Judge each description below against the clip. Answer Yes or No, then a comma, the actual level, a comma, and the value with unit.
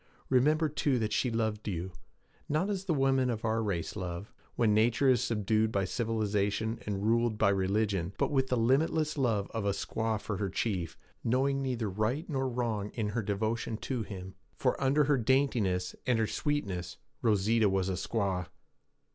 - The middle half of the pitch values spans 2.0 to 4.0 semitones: No, average, 4.4 semitones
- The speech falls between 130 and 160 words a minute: No, average, 175 wpm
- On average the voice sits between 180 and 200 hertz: No, low, 110 Hz